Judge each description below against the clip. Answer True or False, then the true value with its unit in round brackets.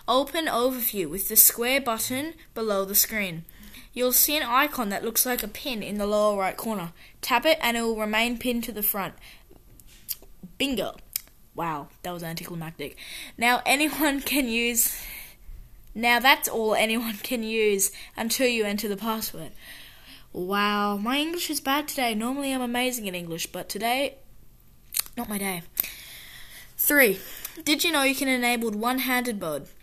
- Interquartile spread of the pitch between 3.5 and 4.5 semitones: True (3.9 semitones)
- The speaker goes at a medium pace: True (160 wpm)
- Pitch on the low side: False (230 Hz)